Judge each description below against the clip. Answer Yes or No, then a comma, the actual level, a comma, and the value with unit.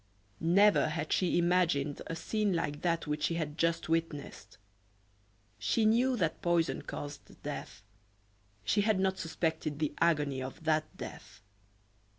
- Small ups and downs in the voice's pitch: No, average, 3.3 semitones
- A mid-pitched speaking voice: Yes, medium, 165 Hz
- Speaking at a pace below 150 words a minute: Yes, average, 140 wpm